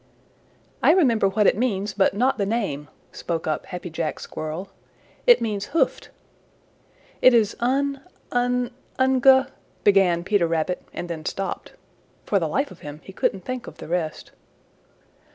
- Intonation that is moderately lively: No, wide, 6.3 semitones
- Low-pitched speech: No, high, 200 Hz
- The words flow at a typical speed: Yes, average, 155 wpm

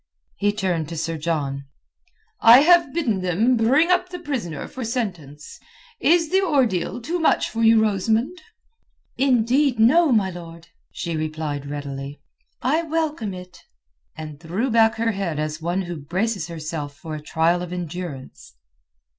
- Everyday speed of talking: Yes, average, 150 wpm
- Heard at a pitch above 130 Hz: Yes, high, 190 Hz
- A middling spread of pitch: No, wide, 7.8 semitones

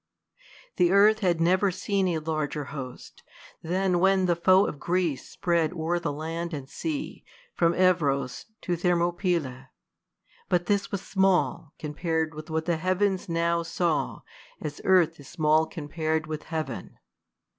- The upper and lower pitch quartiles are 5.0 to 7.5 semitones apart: No, average, 2.8 semitones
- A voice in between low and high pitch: Yes, medium, 170 Hz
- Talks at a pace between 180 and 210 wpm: No, average, 150 wpm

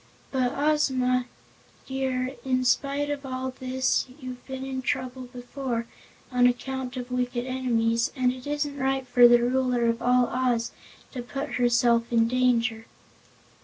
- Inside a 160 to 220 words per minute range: No, average, 145 wpm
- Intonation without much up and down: Yes, narrow, 1.3 semitones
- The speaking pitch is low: No, very high, 255 Hz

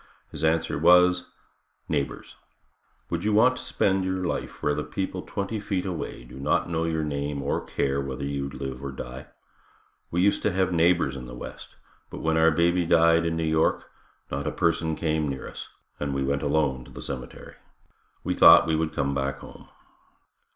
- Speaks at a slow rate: No, average, 190 wpm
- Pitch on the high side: No, very low, 80 Hz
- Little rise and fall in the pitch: No, average, 4.1 semitones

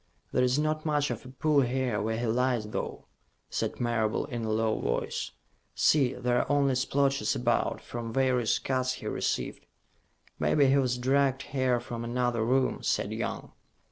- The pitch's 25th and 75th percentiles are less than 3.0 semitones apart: Yes, narrow, 2.4 semitones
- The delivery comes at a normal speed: Yes, average, 170 wpm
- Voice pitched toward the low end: Yes, low, 125 Hz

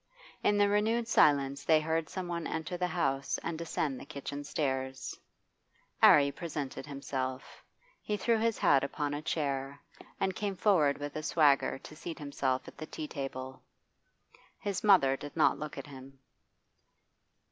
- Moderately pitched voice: Yes, medium, 150 Hz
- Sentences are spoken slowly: No, average, 160 wpm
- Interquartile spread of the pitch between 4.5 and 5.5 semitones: No, average, 3.9 semitones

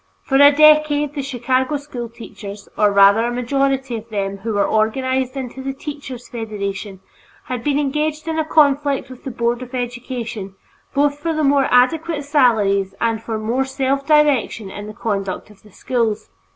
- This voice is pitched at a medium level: No, very high, 250 Hz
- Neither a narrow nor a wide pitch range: Yes, average, 4.4 semitones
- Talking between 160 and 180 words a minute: Yes, average, 170 wpm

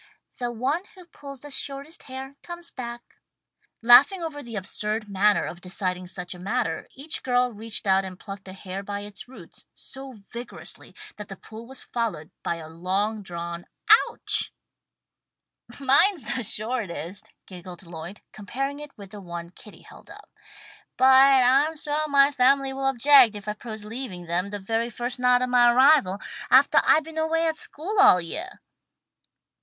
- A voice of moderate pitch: No, high, 235 Hz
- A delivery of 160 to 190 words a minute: Yes, average, 170 wpm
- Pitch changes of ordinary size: No, wide, 5.9 semitones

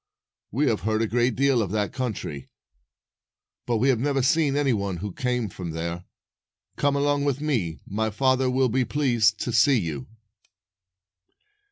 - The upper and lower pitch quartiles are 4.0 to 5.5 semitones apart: Yes, average, 4.6 semitones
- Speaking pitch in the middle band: No, low, 120 Hz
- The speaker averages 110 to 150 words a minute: No, average, 165 wpm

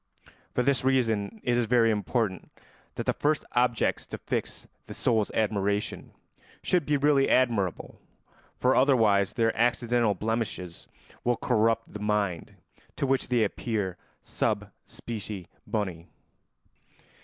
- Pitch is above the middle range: No, low, 115 Hz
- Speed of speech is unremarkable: No, slow, 125 wpm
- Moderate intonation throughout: Yes, average, 3.3 semitones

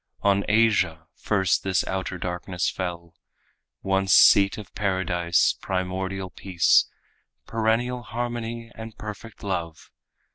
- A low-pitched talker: Yes, very low, 95 Hz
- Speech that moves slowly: Yes, slow, 105 wpm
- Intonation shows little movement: No, average, 3.5 semitones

